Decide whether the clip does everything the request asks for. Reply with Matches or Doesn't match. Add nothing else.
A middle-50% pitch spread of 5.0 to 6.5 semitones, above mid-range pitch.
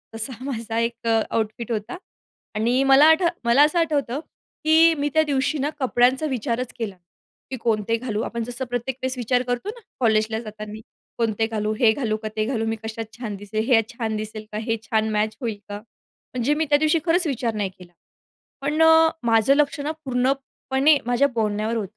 Doesn't match